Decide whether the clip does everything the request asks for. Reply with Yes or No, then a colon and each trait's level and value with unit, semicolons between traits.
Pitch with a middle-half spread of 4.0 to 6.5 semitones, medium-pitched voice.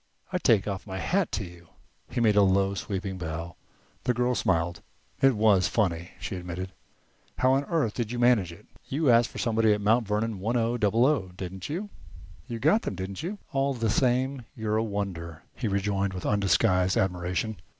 No: average, 4.4 semitones; low, 105 Hz